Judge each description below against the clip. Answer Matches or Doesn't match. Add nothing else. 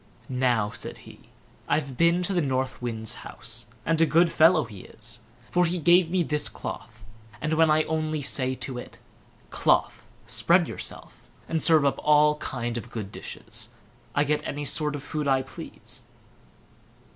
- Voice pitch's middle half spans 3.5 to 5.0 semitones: Matches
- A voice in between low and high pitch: Matches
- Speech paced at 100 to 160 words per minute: Doesn't match